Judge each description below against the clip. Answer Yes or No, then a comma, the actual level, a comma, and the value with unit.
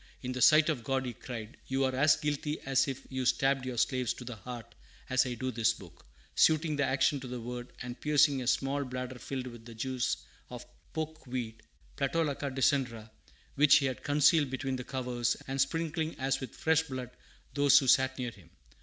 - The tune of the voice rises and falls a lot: No, narrow, 2.4 semitones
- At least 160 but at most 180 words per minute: No, average, 200 wpm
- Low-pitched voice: Yes, low, 130 Hz